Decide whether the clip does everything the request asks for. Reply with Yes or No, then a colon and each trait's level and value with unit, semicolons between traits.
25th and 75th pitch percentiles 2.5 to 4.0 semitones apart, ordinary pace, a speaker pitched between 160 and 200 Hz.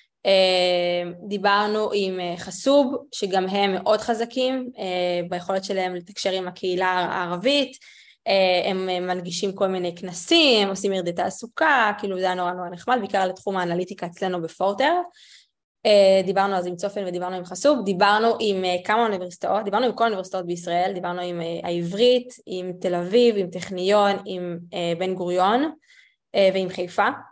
Yes: average, 3.0 semitones; average, 135 wpm; high, 190 Hz